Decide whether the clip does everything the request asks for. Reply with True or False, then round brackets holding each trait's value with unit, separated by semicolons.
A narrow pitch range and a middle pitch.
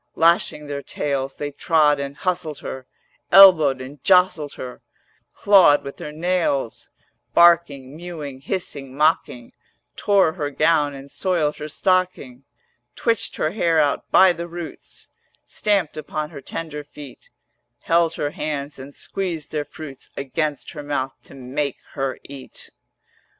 False (3.5 semitones; 150 Hz)